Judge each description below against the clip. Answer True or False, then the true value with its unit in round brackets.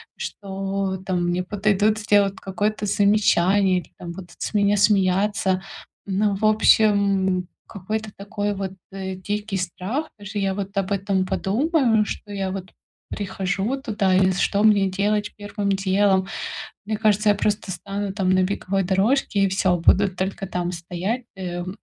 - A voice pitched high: True (195 Hz)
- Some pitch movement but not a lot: False (1.7 semitones)